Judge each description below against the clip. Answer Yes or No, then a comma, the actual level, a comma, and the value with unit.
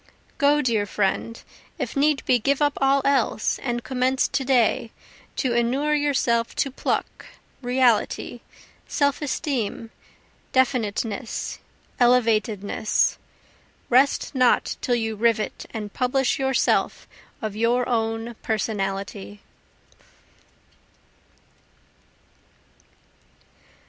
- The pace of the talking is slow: Yes, slow, 90 wpm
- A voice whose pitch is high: Yes, high, 240 Hz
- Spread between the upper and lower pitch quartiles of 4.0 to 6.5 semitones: No, average, 3.2 semitones